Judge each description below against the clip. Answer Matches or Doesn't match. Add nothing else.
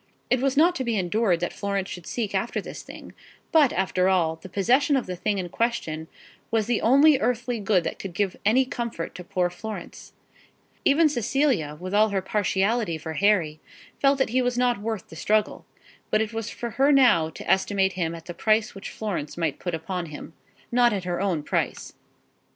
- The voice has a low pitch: Doesn't match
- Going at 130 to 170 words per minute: Doesn't match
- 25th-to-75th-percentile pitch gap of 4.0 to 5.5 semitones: Matches